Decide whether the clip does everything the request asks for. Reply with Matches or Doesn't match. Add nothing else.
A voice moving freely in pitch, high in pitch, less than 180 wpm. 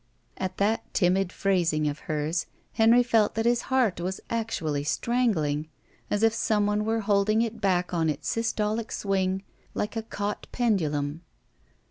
Doesn't match